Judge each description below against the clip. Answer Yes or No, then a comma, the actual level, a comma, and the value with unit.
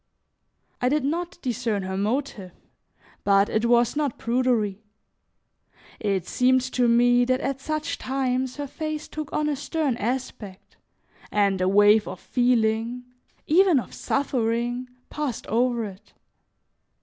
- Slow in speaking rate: Yes, slow, 130 wpm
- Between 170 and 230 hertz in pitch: No, high, 245 Hz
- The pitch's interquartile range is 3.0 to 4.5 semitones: Yes, average, 3.9 semitones